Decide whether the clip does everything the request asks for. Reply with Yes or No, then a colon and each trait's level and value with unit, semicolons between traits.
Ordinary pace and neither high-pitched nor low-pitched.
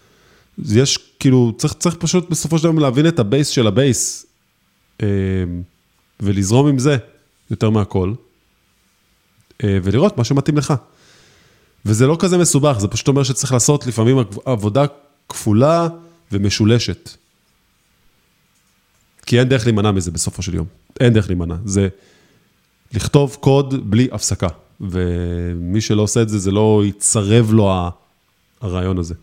No: average, 125 wpm; low, 110 Hz